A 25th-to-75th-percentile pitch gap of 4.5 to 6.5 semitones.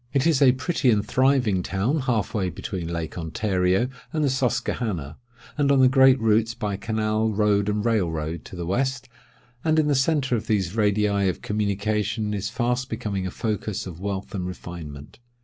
Yes: average, 5.0 semitones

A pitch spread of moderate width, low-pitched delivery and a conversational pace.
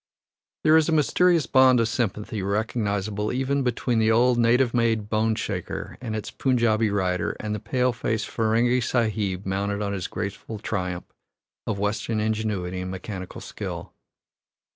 Yes: average, 3.0 semitones; low, 110 Hz; average, 150 wpm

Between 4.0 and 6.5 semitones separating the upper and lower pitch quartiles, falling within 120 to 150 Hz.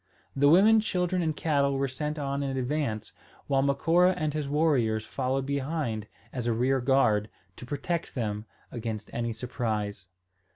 Yes: average, 4.4 semitones; low, 135 Hz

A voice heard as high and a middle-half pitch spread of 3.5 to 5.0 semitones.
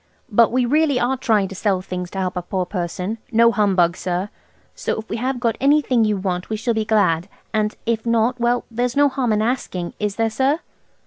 Yes: high, 220 Hz; average, 4.1 semitones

